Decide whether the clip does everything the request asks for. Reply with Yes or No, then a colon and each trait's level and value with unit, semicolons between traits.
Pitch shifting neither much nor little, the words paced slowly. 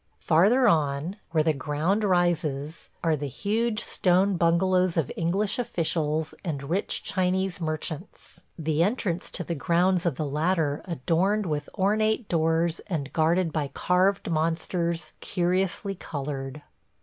Yes: average, 3.3 semitones; slow, 130 wpm